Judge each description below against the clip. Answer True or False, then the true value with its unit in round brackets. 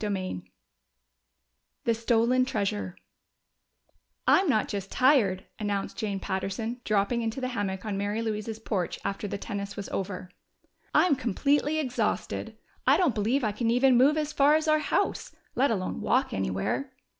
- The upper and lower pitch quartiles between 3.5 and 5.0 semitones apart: True (4.6 semitones)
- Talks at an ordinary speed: True (155 wpm)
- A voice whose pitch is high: True (220 Hz)